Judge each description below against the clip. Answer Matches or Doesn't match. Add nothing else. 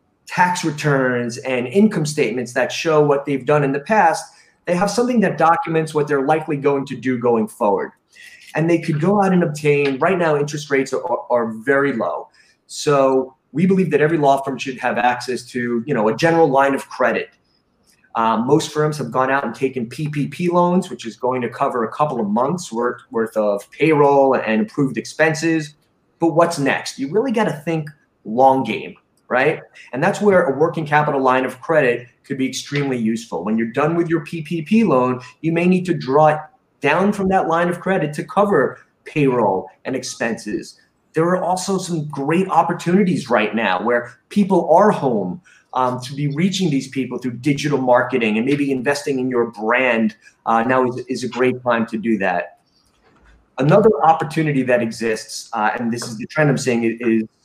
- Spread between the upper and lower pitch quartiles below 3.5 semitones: Doesn't match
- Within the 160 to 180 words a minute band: Doesn't match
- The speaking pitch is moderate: Matches